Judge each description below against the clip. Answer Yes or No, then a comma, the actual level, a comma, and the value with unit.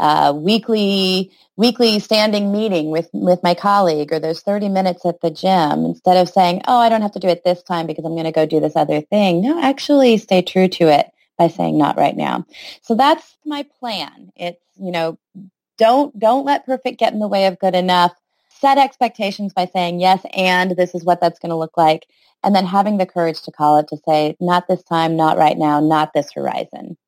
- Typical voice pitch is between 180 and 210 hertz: Yes, medium, 185 Hz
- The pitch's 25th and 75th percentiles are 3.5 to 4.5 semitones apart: Yes, average, 4.0 semitones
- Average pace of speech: No, fast, 220 wpm